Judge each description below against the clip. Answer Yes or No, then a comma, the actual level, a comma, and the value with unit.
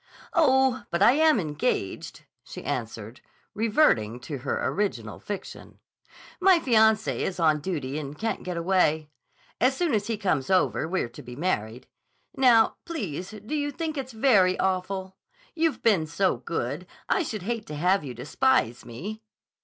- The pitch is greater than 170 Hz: Yes, high, 190 Hz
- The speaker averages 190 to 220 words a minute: No, average, 155 wpm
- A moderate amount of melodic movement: No, wide, 8.2 semitones